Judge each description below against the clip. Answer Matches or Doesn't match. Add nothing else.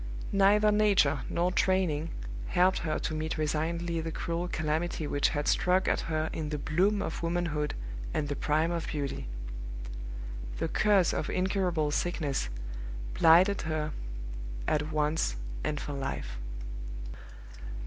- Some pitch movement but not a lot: Matches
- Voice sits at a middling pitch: Matches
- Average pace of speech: Doesn't match